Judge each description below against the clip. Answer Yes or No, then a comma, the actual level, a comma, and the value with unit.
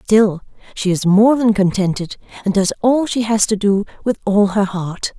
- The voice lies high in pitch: Yes, high, 205 Hz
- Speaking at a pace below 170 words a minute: No, average, 195 wpm